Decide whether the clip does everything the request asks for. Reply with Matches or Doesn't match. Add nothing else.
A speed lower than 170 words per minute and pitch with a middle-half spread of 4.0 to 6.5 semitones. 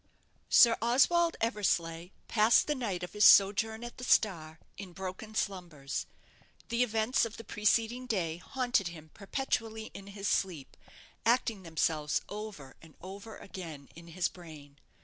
Matches